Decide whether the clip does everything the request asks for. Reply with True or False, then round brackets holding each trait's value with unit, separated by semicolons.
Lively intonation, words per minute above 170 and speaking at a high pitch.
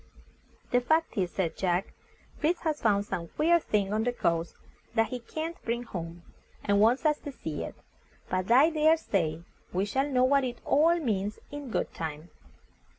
True (7.7 semitones; 180 wpm; 230 Hz)